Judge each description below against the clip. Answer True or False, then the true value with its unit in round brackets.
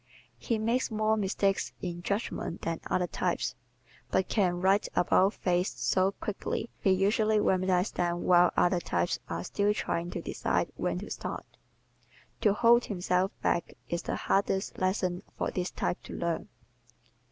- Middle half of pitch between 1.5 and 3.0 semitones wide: True (2.7 semitones)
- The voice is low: False (185 Hz)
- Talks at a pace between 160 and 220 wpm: False (150 wpm)